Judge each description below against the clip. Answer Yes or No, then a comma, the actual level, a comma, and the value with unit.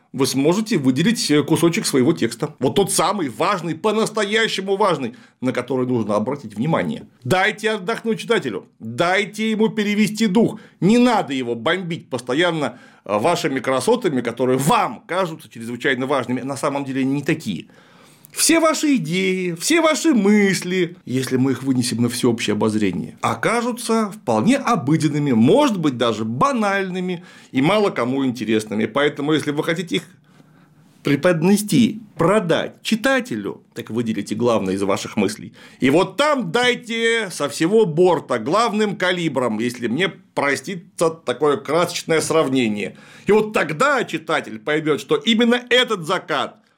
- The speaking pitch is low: No, medium, 170 Hz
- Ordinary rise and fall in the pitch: No, wide, 8.2 semitones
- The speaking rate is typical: Yes, average, 135 wpm